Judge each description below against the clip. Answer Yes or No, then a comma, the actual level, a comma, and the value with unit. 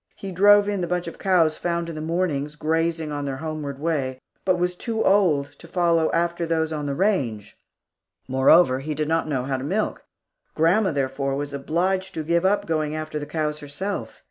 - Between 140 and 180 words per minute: No, average, 195 wpm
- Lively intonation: No, average, 3.6 semitones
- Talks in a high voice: No, medium, 160 Hz